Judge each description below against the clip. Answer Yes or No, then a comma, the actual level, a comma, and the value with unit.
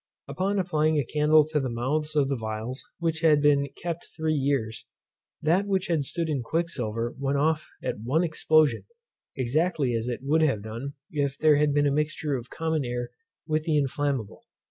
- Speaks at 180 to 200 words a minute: Yes, average, 185 wpm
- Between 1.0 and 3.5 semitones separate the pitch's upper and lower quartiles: Yes, average, 3.2 semitones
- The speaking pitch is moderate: Yes, medium, 145 Hz